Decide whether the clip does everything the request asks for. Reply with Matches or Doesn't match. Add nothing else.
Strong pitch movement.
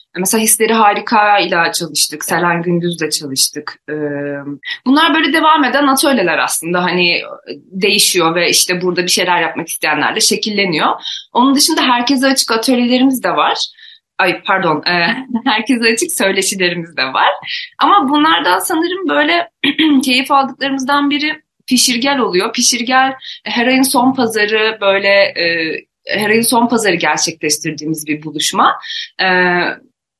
Matches